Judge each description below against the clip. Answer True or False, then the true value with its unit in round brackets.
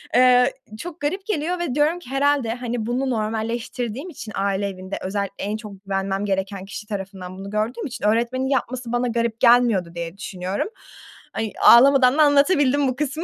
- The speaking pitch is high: True (235 Hz)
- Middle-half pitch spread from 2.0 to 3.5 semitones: False (5.3 semitones)